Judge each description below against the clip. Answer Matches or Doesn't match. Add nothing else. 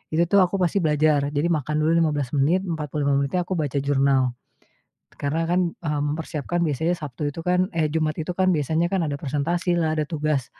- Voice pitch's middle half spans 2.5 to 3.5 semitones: Matches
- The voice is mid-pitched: Matches